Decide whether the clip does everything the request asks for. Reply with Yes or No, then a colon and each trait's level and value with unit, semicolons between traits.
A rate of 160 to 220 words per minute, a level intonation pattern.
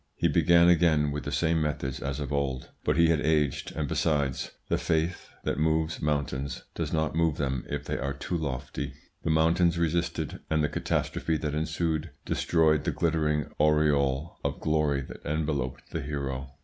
Yes: average, 175 wpm; narrow, 2.3 semitones